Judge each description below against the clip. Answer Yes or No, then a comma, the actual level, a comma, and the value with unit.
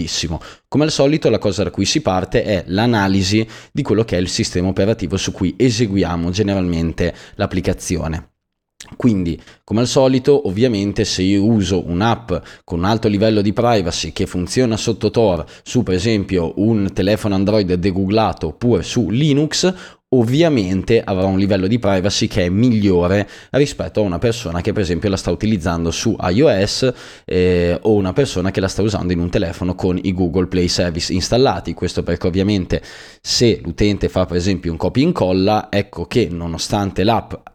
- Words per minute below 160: No, fast, 170 wpm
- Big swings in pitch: No, average, 3.6 semitones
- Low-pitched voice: Yes, low, 100 Hz